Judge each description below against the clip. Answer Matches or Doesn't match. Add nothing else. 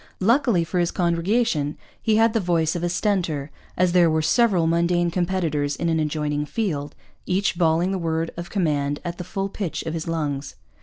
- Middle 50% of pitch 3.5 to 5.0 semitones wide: Doesn't match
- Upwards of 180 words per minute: Matches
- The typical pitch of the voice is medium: Matches